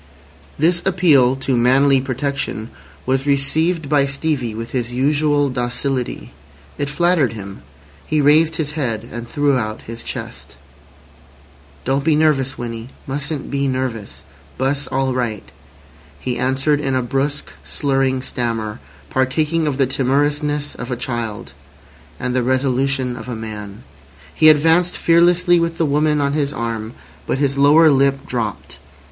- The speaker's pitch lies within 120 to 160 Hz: Yes, low, 135 Hz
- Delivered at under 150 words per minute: Yes, average, 140 wpm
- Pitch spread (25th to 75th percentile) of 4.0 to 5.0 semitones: No, average, 3.2 semitones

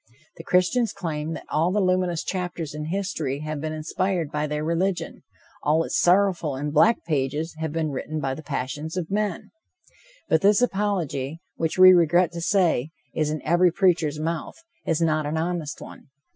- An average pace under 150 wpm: No, average, 175 wpm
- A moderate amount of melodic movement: Yes, average, 3.1 semitones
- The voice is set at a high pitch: No, medium, 165 Hz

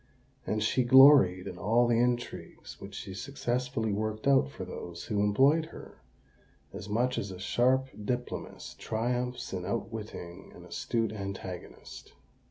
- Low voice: Yes, low, 115 Hz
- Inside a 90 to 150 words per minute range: Yes, average, 140 wpm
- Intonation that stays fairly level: No, average, 3.9 semitones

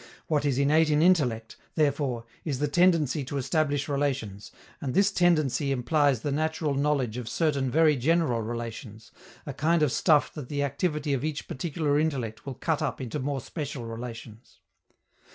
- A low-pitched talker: No, medium, 145 Hz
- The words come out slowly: No, average, 165 wpm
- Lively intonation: No, average, 3.7 semitones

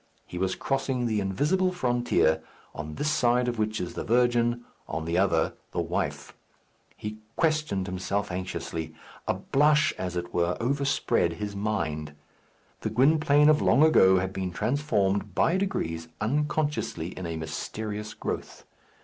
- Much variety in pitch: Yes, wide, 7.4 semitones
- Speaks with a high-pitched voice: No, low, 105 Hz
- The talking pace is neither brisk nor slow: Yes, average, 145 wpm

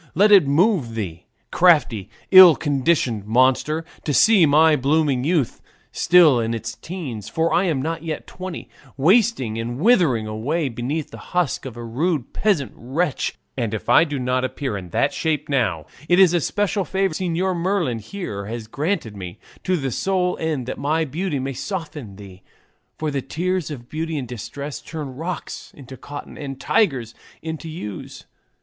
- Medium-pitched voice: Yes, medium, 150 Hz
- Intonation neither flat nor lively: No, wide, 6.0 semitones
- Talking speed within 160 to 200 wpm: Yes, average, 170 wpm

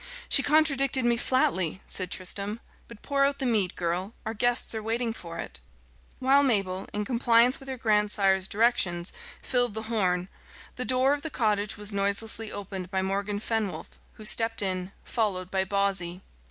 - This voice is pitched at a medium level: No, high, 210 Hz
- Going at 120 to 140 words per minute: No, average, 165 wpm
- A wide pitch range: No, average, 4.0 semitones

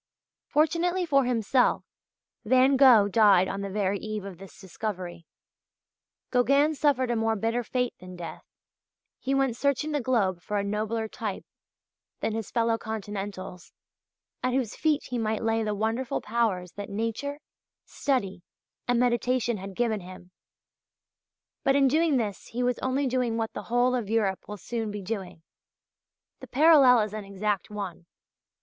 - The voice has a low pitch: No, high, 225 Hz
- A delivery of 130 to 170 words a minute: Yes, average, 155 wpm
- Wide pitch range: No, average, 4.1 semitones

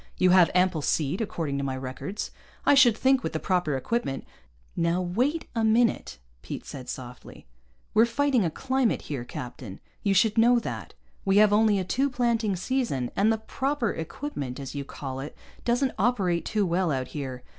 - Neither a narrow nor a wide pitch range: No, wide, 8.8 semitones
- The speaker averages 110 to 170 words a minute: No, average, 185 wpm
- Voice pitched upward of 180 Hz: Yes, high, 190 Hz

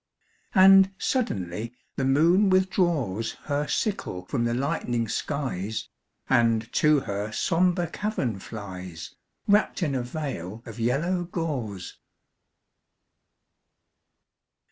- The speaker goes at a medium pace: No, slow, 100 wpm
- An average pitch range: No, wide, 7.9 semitones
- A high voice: No, low, 135 Hz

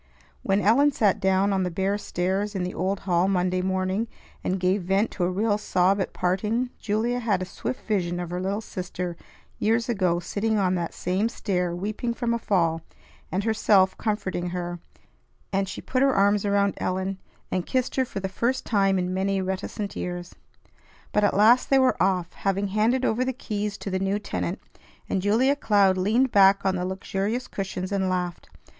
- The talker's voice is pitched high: Yes, high, 195 Hz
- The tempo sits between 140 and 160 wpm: No, average, 190 wpm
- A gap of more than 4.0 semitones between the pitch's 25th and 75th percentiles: No, narrow, 2.6 semitones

